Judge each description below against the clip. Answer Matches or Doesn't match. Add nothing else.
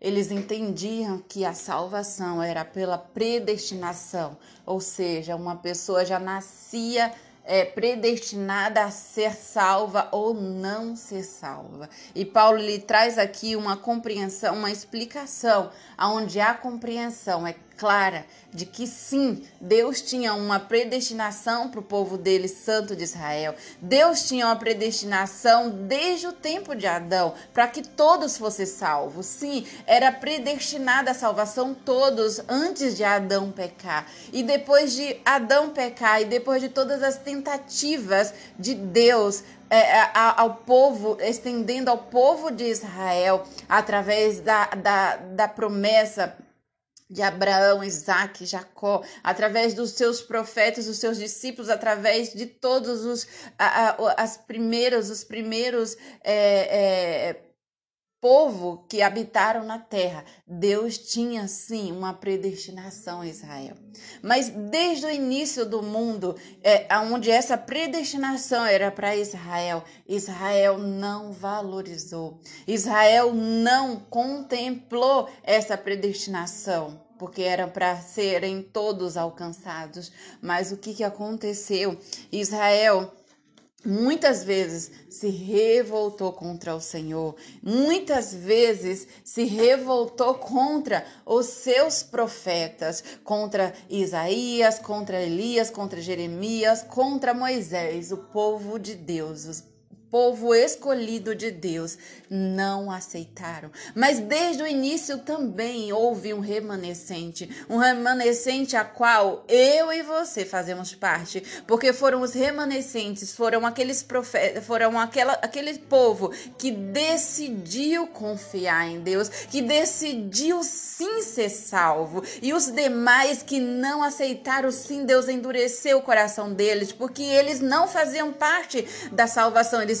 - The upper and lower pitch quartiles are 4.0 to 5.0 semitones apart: Matches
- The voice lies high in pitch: Matches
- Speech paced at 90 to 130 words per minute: Matches